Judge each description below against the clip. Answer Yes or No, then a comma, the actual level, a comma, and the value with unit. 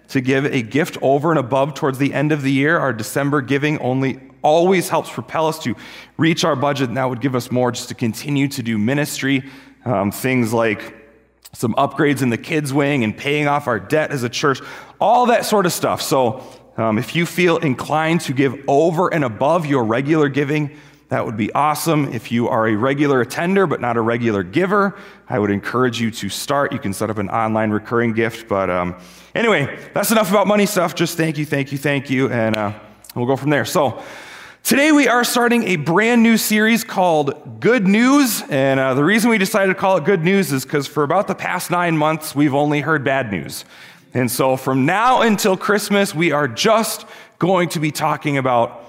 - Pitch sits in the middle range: Yes, medium, 145 Hz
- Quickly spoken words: Yes, fast, 210 wpm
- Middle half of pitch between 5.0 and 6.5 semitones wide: Yes, wide, 5.6 semitones